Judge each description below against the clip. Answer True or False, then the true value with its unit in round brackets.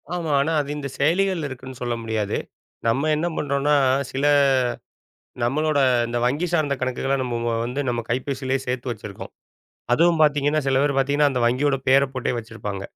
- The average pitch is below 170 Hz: True (135 Hz)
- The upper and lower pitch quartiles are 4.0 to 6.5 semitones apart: False (3.2 semitones)